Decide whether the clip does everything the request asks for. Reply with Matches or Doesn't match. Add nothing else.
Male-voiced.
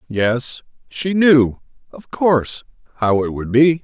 Matches